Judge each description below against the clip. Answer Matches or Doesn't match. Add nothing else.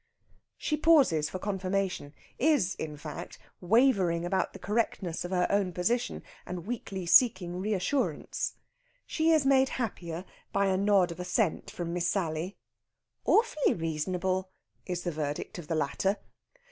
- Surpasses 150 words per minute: Doesn't match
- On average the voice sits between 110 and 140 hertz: Doesn't match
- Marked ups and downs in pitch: Doesn't match